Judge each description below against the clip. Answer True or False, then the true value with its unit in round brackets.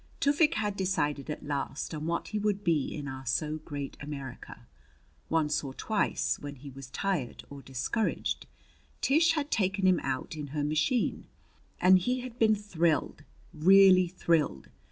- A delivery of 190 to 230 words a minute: False (155 wpm)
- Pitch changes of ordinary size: False (6.0 semitones)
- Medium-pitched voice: True (165 Hz)